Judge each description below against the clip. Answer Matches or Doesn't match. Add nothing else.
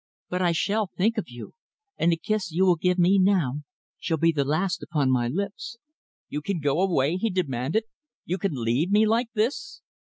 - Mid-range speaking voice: Matches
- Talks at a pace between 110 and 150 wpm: Doesn't match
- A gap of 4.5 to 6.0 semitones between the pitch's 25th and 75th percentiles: Matches